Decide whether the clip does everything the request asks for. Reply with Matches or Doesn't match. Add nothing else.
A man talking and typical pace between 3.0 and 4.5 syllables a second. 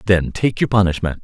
Doesn't match